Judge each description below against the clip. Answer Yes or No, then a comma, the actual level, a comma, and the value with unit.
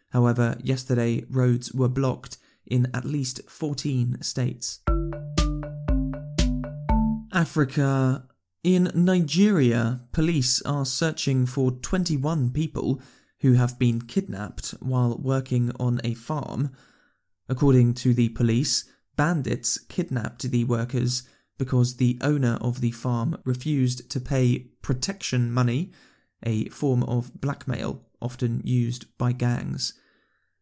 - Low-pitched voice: Yes, low, 125 Hz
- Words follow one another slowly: Yes, slow, 110 wpm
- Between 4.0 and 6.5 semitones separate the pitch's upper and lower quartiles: No, average, 2.7 semitones